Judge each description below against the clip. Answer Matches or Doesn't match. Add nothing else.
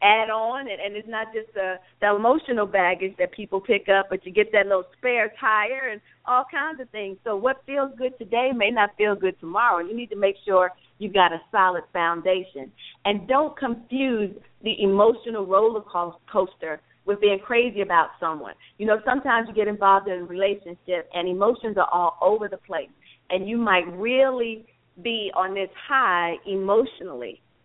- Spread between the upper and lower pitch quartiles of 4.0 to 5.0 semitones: Doesn't match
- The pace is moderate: Matches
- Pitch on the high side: Matches